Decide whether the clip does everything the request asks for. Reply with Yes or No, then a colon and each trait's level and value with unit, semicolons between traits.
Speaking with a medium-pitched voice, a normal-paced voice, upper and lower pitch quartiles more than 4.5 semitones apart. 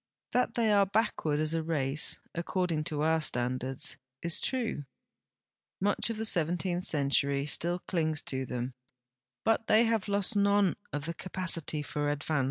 Yes: medium, 165 Hz; average, 155 wpm; wide, 5.4 semitones